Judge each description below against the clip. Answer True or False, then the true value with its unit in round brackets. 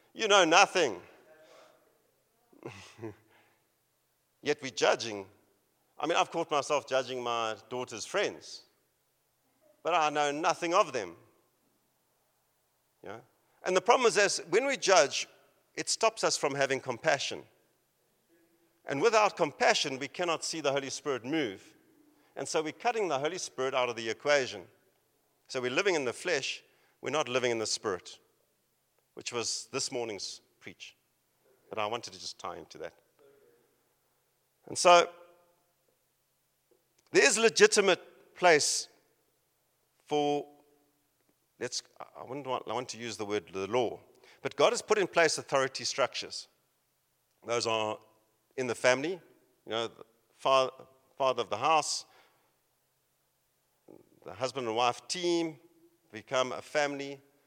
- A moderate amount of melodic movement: False (5.7 semitones)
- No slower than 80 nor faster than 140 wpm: True (135 wpm)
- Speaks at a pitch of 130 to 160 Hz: True (140 Hz)